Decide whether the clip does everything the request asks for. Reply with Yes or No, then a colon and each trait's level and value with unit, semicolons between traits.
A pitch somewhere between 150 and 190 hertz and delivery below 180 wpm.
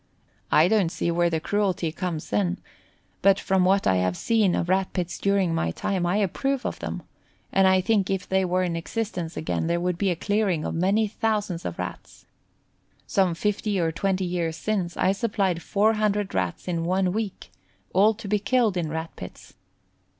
No: medium, 185 Hz; average, 185 wpm